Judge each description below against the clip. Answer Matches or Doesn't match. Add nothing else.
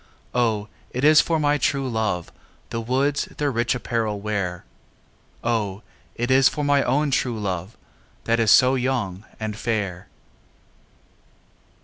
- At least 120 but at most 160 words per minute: Matches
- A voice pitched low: Matches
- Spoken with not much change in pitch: Doesn't match